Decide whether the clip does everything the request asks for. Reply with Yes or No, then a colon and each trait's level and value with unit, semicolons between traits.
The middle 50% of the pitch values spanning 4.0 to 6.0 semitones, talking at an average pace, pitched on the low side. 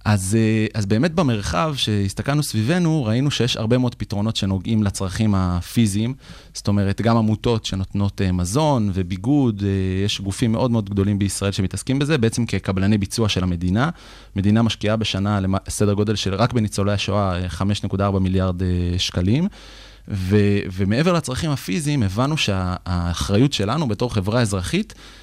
No: average, 3.1 semitones; average, 140 wpm; low, 105 Hz